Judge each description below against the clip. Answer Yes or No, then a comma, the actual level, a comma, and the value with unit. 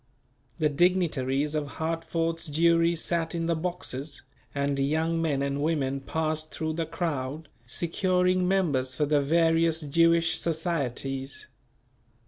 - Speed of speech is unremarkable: No, slow, 120 wpm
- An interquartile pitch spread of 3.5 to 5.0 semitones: No, average, 2.8 semitones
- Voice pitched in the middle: Yes, medium, 160 Hz